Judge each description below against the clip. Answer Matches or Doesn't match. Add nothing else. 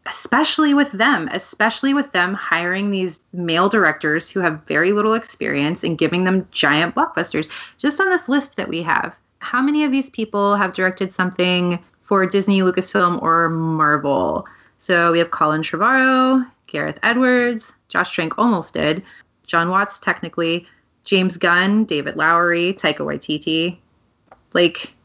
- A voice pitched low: Doesn't match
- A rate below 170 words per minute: Matches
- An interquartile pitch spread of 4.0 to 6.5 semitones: Matches